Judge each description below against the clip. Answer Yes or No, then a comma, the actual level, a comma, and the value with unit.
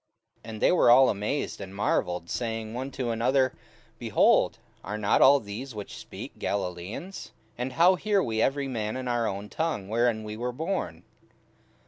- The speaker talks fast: No, average, 175 wpm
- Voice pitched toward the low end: Yes, low, 115 Hz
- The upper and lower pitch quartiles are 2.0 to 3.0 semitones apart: No, average, 4.3 semitones